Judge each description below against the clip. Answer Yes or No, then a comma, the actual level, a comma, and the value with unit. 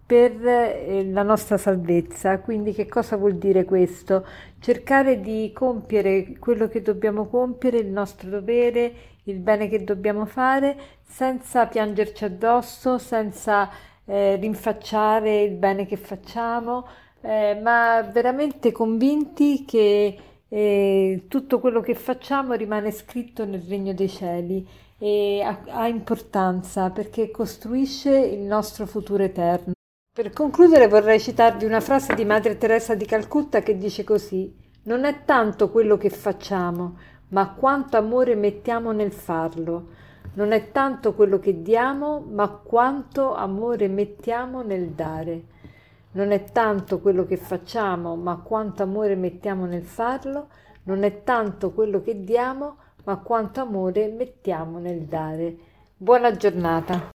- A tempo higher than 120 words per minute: Yes, average, 130 wpm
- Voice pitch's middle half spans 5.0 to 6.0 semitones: No, average, 3.3 semitones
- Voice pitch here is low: No, high, 215 Hz